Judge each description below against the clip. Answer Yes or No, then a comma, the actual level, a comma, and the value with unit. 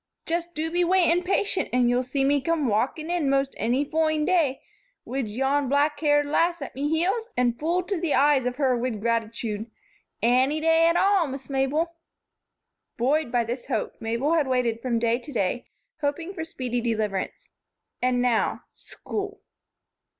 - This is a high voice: Yes, very high, 280 Hz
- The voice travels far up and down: No, average, 4.9 semitones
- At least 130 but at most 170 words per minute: Yes, average, 165 wpm